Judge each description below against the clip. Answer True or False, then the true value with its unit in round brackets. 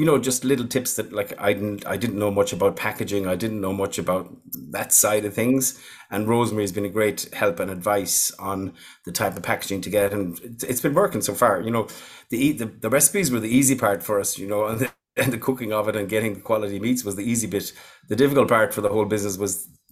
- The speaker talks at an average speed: False (245 wpm)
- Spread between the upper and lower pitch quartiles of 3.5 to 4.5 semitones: False (3.1 semitones)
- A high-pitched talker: False (105 Hz)